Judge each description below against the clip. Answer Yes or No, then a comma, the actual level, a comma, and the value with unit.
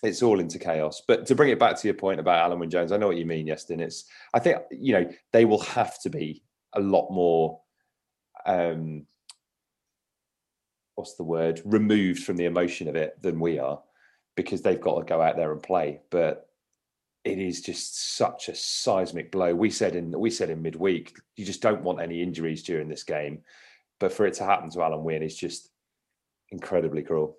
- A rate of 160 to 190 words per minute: No, fast, 205 wpm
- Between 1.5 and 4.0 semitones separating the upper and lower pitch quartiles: Yes, narrow, 2.4 semitones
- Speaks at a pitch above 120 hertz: No, very low, 85 Hz